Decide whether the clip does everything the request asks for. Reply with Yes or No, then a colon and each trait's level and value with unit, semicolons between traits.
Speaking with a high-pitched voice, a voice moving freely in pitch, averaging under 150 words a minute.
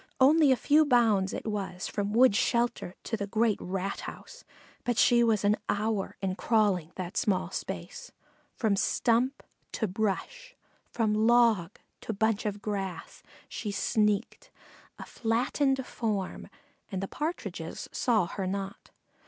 No: high, 215 Hz; average, 3.3 semitones; average, 140 wpm